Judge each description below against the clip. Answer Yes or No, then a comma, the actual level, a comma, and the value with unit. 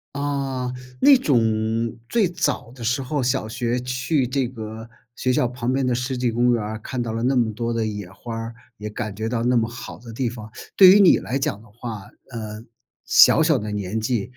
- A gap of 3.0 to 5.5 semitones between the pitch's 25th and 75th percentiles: No, narrow, 2.6 semitones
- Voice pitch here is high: No, low, 120 Hz